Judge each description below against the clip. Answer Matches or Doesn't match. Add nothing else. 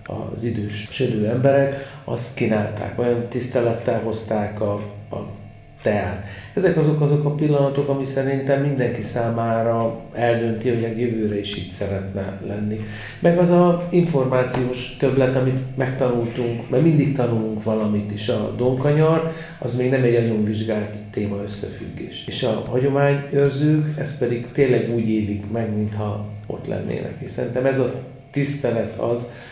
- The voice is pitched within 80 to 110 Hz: Doesn't match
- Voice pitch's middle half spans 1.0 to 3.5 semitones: Doesn't match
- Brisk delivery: Doesn't match